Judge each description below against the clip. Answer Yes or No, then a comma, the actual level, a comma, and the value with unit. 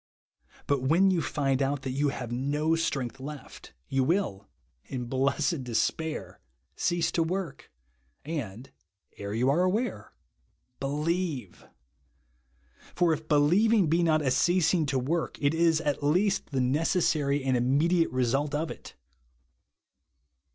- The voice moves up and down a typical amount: Yes, average, 4.0 semitones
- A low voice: No, medium, 145 Hz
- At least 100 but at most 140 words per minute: Yes, slow, 135 wpm